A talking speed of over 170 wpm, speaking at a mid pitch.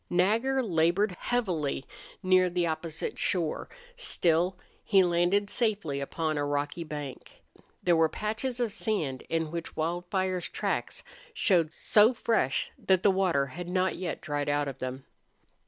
No: average, 140 wpm; medium, 175 Hz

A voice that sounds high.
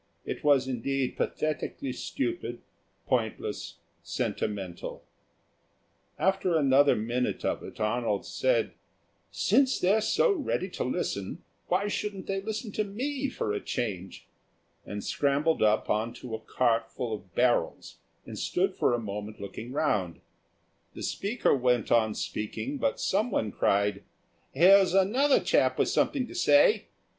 No: low, 135 Hz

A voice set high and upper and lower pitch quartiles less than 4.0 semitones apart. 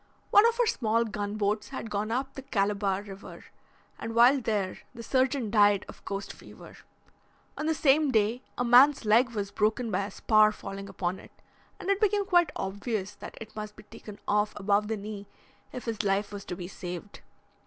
Yes: high, 215 Hz; average, 3.6 semitones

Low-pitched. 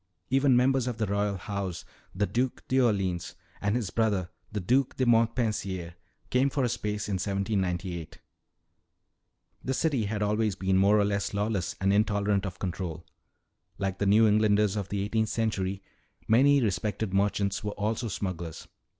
Yes: low, 105 Hz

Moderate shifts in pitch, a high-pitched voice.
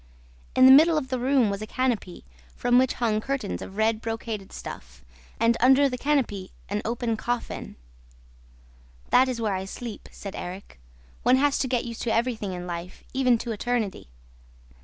Yes: average, 3.6 semitones; high, 235 Hz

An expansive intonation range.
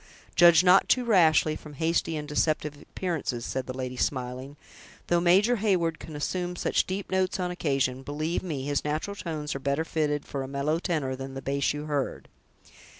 No: average, 4.0 semitones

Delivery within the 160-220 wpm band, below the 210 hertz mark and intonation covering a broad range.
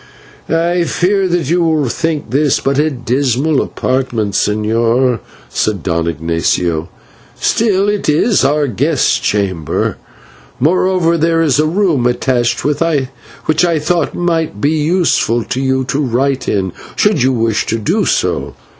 No: average, 140 wpm; medium, 140 Hz; wide, 5.9 semitones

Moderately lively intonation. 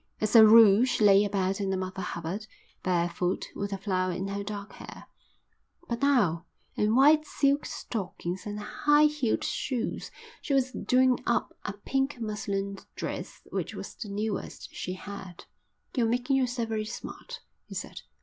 Yes: average, 4.2 semitones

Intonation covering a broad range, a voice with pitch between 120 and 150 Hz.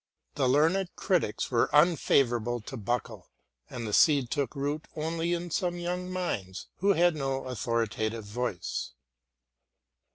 Yes: wide, 6.5 semitones; low, 135 Hz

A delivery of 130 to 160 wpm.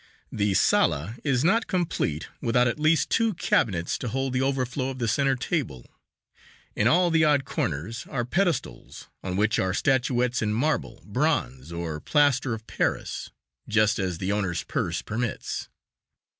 Yes: average, 155 wpm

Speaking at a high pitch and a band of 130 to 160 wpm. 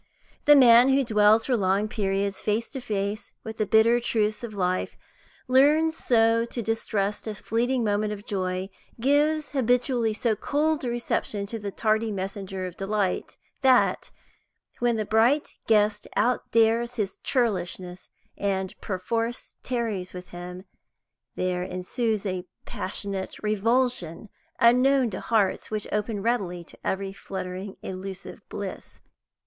Yes: high, 215 Hz; slow, 135 wpm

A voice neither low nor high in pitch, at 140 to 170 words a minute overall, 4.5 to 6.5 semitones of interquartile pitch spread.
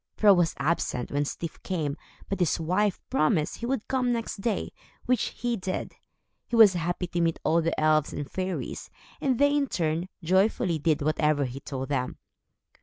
No: medium, 175 Hz; average, 180 wpm; average, 5.3 semitones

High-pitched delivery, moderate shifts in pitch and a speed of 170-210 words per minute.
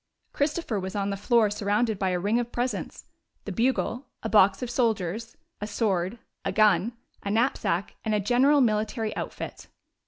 Yes: high, 215 Hz; average, 3.2 semitones; average, 175 wpm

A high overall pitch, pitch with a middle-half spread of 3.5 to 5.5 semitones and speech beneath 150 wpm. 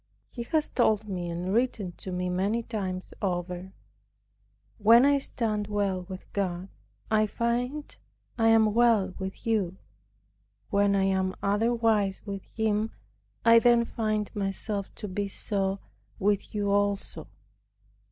No: high, 205 Hz; average, 2.9 semitones; slow, 135 wpm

